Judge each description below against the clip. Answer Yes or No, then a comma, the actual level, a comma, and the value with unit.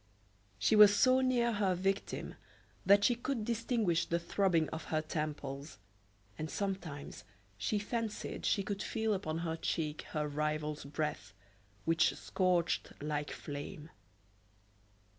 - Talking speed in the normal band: No, slow, 125 wpm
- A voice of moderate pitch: Yes, medium, 170 Hz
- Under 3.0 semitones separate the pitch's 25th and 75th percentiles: No, average, 5.3 semitones